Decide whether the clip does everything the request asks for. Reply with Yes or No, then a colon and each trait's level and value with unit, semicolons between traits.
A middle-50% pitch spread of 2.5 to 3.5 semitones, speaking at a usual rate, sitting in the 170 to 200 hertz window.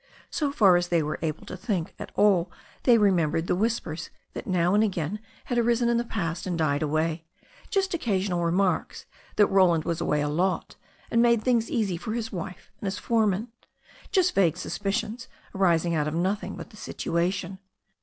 No: average, 4.7 semitones; average, 190 wpm; high, 190 Hz